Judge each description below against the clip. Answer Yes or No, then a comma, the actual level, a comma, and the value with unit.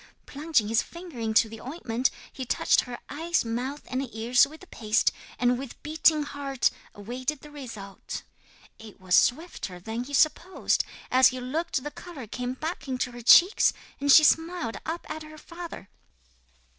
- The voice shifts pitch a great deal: No, average, 4.8 semitones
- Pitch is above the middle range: Yes, very high, 260 Hz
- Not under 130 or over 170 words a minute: Yes, average, 165 wpm